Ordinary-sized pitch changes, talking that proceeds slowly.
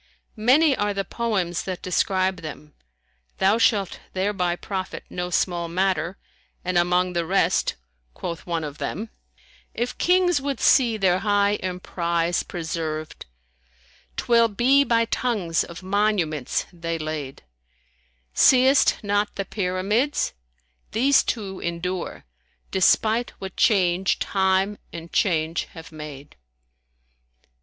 Yes: average, 3.8 semitones; slow, 120 wpm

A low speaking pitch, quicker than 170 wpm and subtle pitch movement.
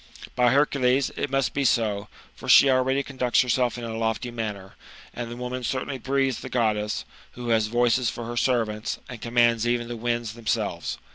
Yes: low, 120 Hz; average, 190 wpm; narrow, 2.0 semitones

